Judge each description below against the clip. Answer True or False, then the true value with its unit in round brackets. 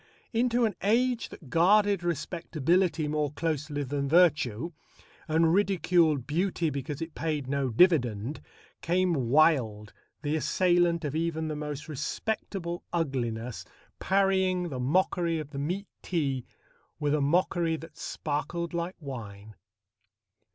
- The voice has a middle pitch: True (160 Hz)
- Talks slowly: True (125 wpm)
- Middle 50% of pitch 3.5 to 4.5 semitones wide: True (3.9 semitones)